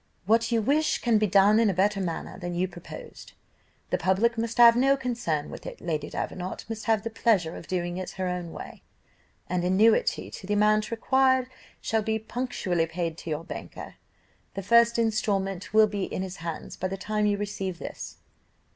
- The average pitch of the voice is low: No, high, 205 Hz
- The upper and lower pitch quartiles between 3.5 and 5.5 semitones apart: Yes, average, 4.0 semitones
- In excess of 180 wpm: Yes, average, 190 wpm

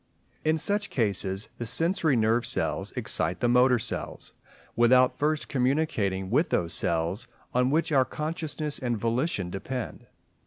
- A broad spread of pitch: Yes, wide, 5.7 semitones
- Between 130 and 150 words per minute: Yes, average, 140 wpm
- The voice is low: Yes, low, 125 Hz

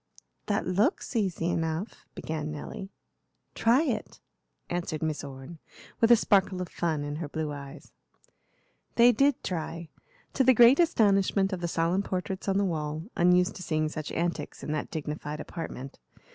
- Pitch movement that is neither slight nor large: Yes, average, 4.5 semitones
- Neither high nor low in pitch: Yes, medium, 175 Hz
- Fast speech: No, average, 160 wpm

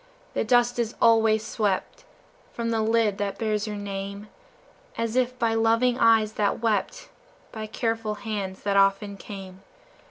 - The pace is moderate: Yes, average, 150 wpm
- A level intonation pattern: Yes, narrow, 2.1 semitones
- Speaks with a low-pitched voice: No, high, 220 Hz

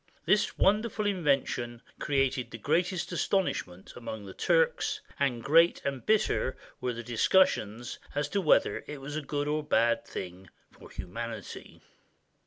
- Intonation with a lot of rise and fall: Yes, wide, 7.5 semitones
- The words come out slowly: No, average, 145 wpm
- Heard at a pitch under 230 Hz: Yes, medium, 140 Hz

